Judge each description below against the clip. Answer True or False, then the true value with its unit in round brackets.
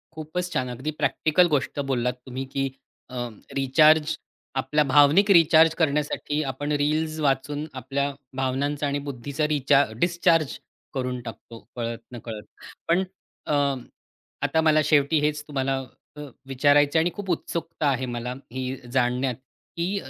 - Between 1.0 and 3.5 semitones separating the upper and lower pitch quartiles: True (3.0 semitones)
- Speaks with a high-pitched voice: False (145 Hz)